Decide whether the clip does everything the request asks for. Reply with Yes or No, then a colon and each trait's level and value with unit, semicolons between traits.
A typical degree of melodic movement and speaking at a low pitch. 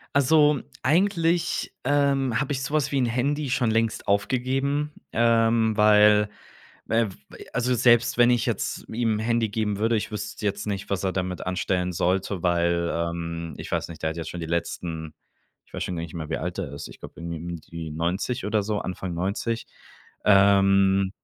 No: wide, 5.7 semitones; low, 105 Hz